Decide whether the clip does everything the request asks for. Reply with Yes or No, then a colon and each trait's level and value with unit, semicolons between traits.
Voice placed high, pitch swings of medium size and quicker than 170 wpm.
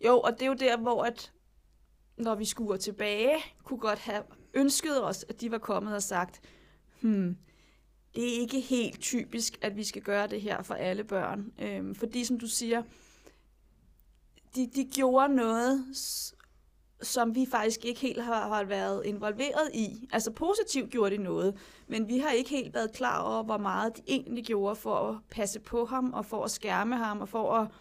Yes: high, 225 Hz; average, 3.0 semitones; average, 190 wpm